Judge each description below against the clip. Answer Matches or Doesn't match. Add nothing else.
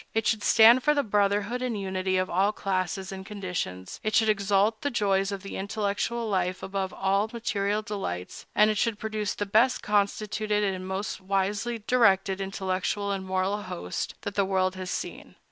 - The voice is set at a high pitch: Matches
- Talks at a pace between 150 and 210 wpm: Matches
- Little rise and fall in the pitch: Matches